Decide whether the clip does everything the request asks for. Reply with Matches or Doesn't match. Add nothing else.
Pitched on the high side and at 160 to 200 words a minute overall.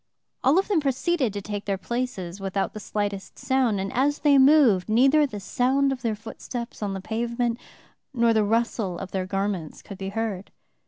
Matches